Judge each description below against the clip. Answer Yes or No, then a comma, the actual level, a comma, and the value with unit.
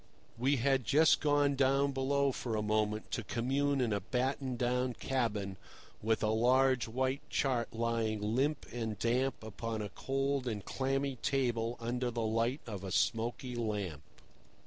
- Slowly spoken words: No, average, 155 wpm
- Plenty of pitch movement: No, average, 3.3 semitones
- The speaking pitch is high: No, low, 120 Hz